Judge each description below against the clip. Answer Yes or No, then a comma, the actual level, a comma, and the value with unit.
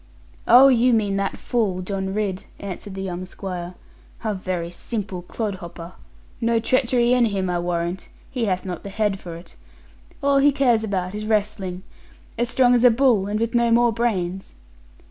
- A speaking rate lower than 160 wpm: No, average, 180 wpm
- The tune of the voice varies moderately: Yes, average, 4.2 semitones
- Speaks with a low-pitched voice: No, high, 205 Hz